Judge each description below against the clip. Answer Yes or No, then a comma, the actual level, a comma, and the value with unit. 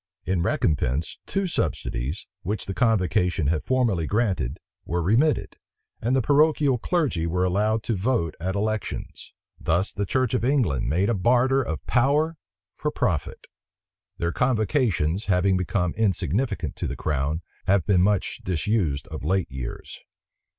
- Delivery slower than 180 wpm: Yes, average, 145 wpm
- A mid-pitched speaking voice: No, low, 100 Hz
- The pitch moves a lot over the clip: Yes, wide, 6.5 semitones